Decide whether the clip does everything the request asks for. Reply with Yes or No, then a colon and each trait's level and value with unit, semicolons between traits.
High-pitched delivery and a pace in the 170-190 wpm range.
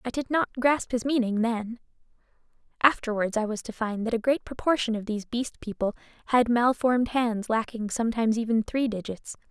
Yes: high, 235 Hz; average, 175 wpm